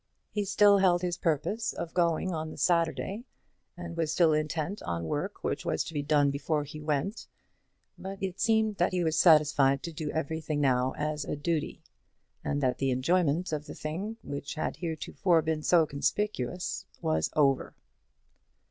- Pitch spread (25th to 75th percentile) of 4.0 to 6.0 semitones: No, average, 3.5 semitones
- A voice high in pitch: No, medium, 160 Hz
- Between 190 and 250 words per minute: No, average, 170 wpm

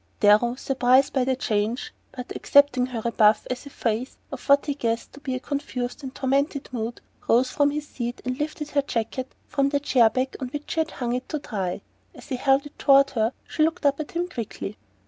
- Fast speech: Yes, fast, 220 wpm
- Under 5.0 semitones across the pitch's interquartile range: Yes, average, 2.9 semitones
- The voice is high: Yes, very high, 260 Hz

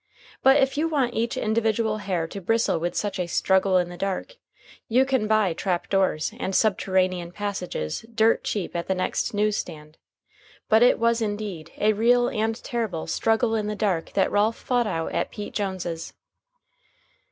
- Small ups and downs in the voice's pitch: No, average, 3.6 semitones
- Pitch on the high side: Yes, high, 205 Hz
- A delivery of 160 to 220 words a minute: Yes, average, 175 wpm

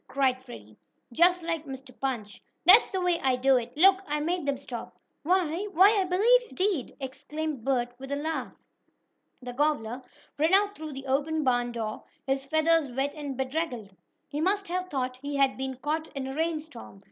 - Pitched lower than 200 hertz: No, very high, 285 Hz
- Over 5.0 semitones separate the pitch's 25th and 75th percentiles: No, average, 4.2 semitones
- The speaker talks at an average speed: Yes, average, 185 wpm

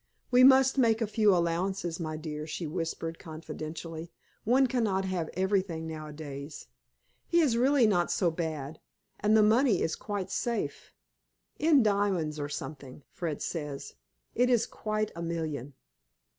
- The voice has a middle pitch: Yes, medium, 175 Hz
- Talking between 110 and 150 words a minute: Yes, average, 145 wpm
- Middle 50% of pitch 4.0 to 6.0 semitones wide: Yes, wide, 5.6 semitones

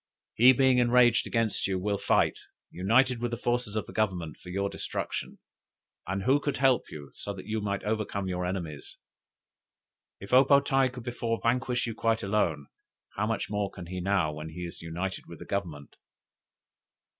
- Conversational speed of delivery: Yes, average, 180 wpm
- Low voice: Yes, low, 105 Hz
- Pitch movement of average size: Yes, average, 4.7 semitones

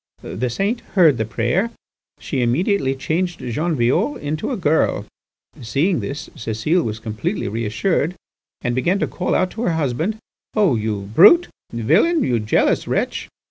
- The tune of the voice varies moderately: No, wide, 7.7 semitones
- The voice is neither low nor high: Yes, medium, 150 Hz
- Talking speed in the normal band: Yes, average, 150 wpm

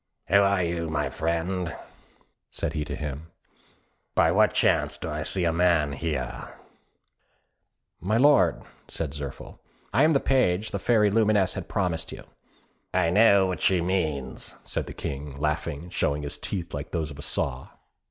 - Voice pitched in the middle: No, very low, 85 Hz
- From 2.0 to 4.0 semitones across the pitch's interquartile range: No, average, 4.5 semitones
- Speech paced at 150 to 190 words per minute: Yes, average, 165 wpm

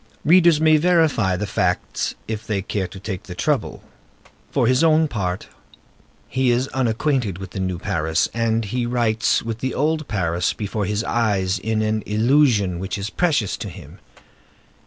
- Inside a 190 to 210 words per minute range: No, average, 165 wpm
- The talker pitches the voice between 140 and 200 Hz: No, low, 110 Hz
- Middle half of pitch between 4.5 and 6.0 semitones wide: Yes, average, 5.2 semitones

